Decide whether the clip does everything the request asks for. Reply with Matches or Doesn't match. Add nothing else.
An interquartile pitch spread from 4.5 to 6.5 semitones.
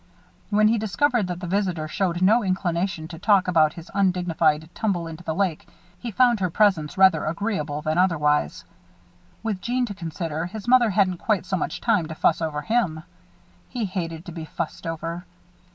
Doesn't match